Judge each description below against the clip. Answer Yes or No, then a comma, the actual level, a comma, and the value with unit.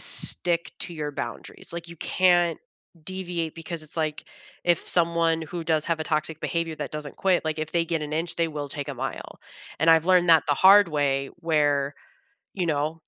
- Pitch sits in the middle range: Yes, medium, 160 Hz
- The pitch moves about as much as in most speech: No, narrow, 2.0 semitones